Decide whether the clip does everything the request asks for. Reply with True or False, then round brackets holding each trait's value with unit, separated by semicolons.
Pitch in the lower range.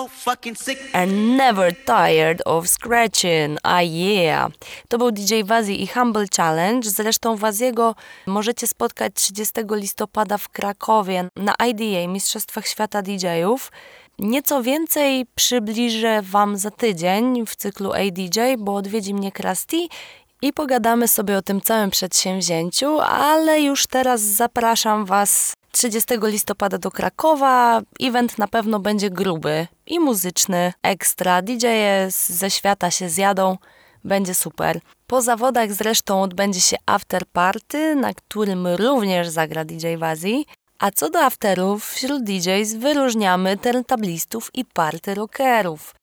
False (215 Hz)